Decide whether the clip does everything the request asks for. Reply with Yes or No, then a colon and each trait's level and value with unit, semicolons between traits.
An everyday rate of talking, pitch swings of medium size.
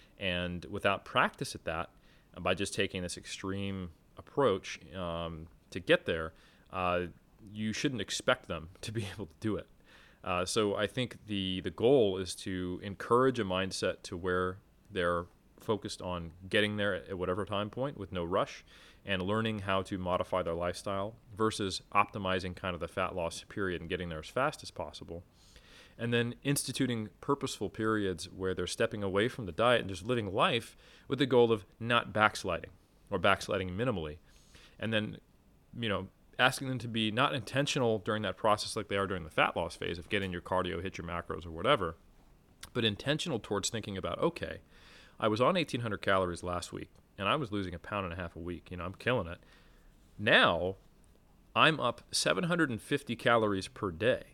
Yes: average, 180 wpm; average, 3.8 semitones